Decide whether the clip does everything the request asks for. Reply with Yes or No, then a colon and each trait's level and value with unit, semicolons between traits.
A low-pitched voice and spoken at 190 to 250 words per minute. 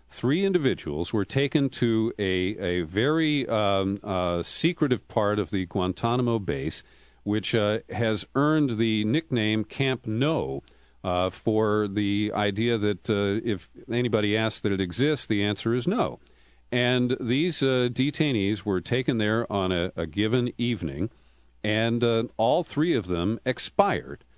No: low, 110 Hz; average, 145 wpm